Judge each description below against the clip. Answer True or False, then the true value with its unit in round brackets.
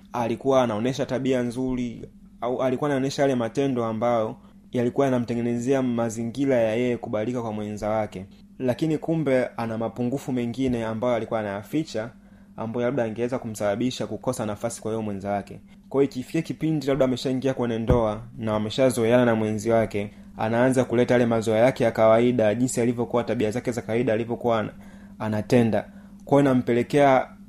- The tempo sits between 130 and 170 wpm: True (135 wpm)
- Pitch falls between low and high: False (120 Hz)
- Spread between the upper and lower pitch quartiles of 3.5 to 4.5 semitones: False (2.9 semitones)